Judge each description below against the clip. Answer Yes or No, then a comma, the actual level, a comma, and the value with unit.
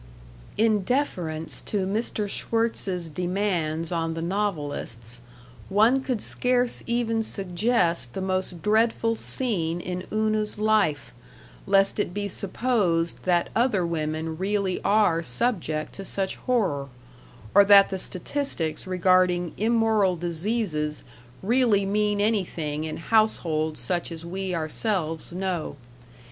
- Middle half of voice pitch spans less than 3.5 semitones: No, average, 4.5 semitones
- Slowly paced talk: Yes, slow, 115 wpm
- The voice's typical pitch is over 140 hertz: Yes, high, 190 Hz